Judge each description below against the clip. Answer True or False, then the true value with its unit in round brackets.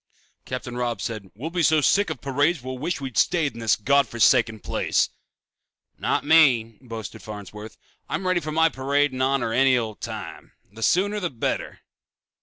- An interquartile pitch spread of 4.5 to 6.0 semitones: True (5.2 semitones)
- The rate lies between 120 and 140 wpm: False (180 wpm)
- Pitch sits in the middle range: False (130 Hz)